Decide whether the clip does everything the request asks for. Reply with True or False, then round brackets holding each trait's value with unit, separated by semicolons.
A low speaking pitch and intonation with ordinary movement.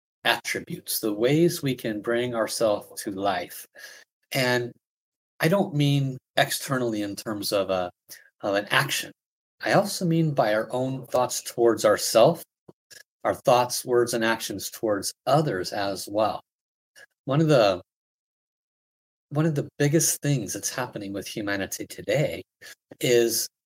True (125 Hz; 4.6 semitones)